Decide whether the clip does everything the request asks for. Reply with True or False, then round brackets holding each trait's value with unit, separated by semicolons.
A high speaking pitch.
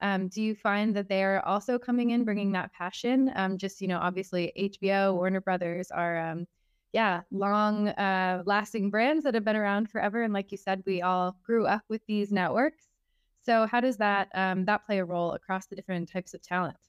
True (195 Hz)